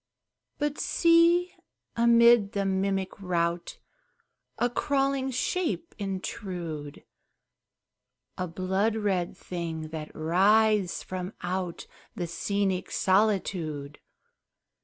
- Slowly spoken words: Yes, slow, 85 wpm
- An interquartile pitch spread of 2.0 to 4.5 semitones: No, average, 4.9 semitones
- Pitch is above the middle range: Yes, high, 195 Hz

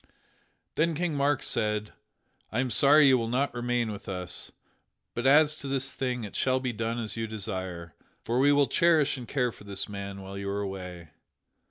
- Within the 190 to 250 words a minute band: Yes, average, 195 wpm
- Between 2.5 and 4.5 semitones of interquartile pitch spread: No, wide, 5.6 semitones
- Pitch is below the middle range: Yes, low, 120 Hz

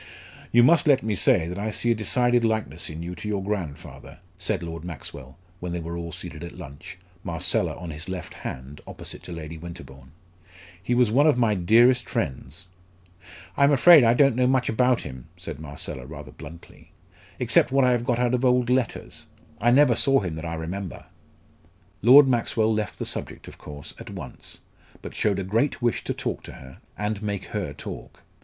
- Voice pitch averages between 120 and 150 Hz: No, low, 100 Hz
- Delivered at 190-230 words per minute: Yes, average, 195 wpm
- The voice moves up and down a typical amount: No, wide, 6.9 semitones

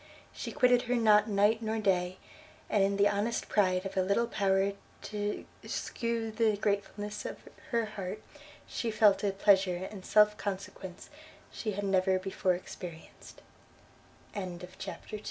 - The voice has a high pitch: Yes, high, 205 Hz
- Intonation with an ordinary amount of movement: No, narrow, 2.2 semitones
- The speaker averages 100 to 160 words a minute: Yes, average, 155 wpm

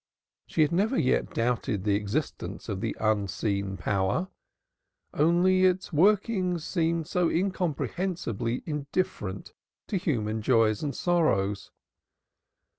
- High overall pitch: No, medium, 150 Hz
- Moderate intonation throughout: No, wide, 9.0 semitones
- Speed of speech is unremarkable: No, slow, 110 wpm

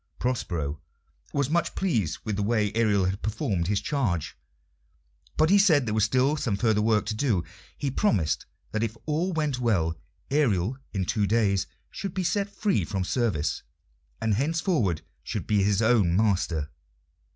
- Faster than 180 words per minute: No, average, 160 wpm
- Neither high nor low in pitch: No, low, 110 Hz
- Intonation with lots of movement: Yes, wide, 6.4 semitones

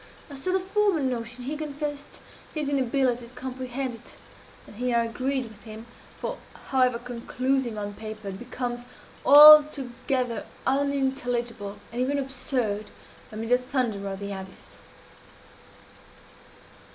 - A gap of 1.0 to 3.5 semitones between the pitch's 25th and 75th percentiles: Yes, average, 2.9 semitones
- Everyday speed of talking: No, slow, 125 wpm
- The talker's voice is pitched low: No, very high, 250 Hz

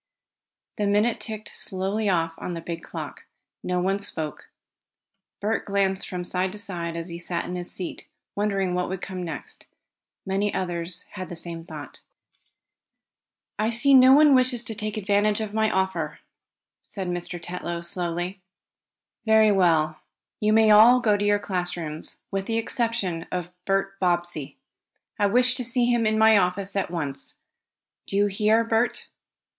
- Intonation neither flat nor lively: Yes, average, 3.5 semitones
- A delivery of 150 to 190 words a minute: Yes, average, 160 wpm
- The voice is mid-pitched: No, high, 195 Hz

